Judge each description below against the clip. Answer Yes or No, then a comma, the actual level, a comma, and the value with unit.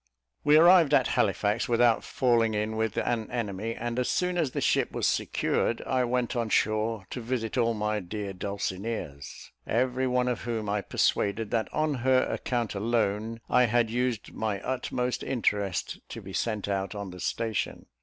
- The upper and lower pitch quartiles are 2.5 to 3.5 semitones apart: Yes, average, 3.0 semitones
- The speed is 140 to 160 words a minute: No, average, 175 wpm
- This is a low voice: Yes, low, 115 Hz